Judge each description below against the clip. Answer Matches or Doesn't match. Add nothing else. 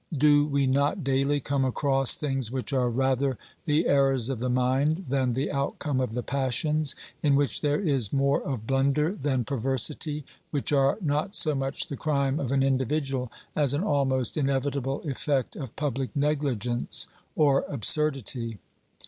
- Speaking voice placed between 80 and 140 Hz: Matches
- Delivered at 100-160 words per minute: Matches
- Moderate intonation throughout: Doesn't match